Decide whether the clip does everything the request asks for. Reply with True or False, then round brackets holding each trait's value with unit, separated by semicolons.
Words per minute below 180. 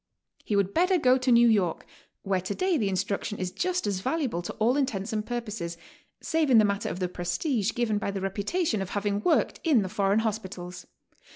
False (200 wpm)